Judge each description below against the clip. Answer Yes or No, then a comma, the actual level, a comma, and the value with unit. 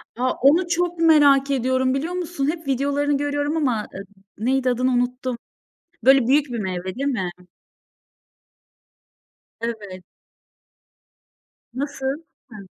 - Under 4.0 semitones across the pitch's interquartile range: Yes, average, 2.8 semitones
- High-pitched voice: Yes, very high, 270 Hz